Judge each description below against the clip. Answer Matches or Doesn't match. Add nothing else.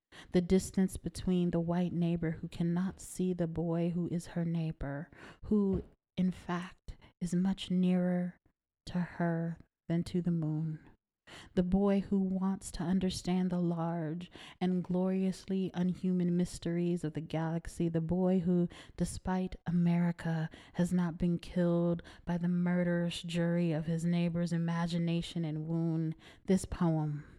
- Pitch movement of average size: Doesn't match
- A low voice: Doesn't match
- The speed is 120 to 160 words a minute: Matches